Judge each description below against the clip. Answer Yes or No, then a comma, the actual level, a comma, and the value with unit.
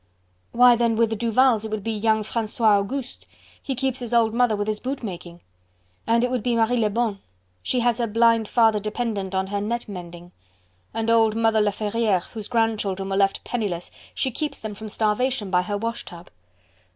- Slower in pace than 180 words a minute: No, average, 190 wpm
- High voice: Yes, high, 220 Hz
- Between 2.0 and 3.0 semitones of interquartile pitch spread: Yes, narrow, 2.4 semitones